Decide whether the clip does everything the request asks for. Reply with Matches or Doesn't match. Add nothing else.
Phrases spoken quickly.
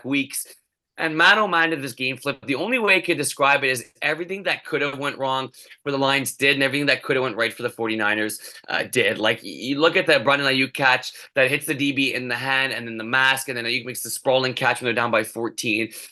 Matches